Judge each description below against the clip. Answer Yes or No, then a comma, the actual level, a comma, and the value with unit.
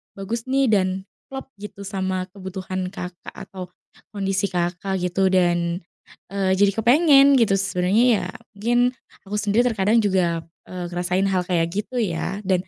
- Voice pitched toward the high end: Yes, high, 195 Hz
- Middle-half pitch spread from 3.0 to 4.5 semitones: No, narrow, 2.5 semitones